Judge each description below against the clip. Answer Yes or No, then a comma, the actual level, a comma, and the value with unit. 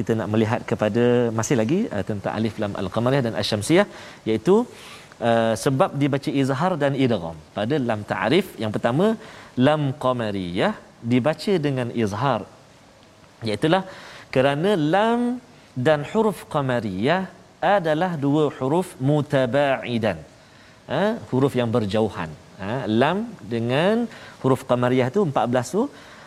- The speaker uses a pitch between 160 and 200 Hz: No, low, 130 Hz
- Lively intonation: Yes, wide, 5.7 semitones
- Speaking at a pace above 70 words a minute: Yes, average, 120 wpm